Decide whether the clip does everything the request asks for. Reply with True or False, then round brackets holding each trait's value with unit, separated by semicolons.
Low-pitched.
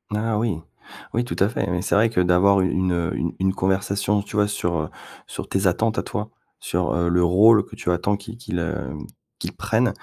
True (95 Hz)